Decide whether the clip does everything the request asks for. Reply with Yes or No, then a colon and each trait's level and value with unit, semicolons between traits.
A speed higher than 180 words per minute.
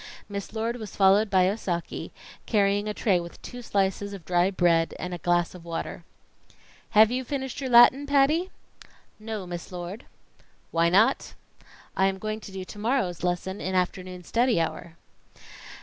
No: average, 165 wpm